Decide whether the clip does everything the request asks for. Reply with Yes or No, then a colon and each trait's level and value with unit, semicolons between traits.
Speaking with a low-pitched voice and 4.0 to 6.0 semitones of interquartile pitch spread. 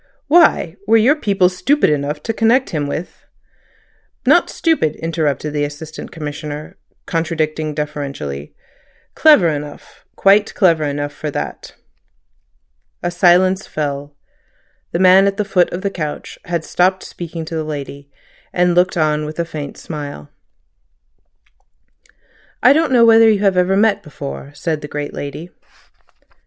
No: medium, 165 Hz; average, 4.5 semitones